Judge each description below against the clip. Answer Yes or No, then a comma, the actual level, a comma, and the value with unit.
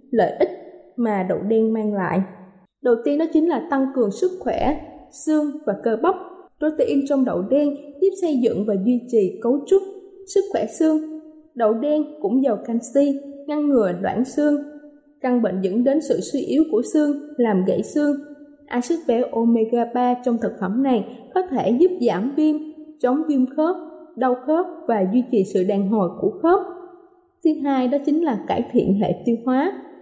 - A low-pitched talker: No, very high, 275 Hz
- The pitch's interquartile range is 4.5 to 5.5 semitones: Yes, average, 5.1 semitones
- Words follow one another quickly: No, average, 180 wpm